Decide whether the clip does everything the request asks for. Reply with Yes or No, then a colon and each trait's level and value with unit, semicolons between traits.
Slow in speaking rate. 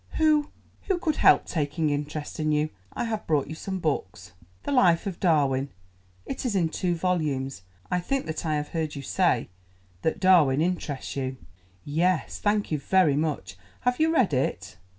No: average, 165 wpm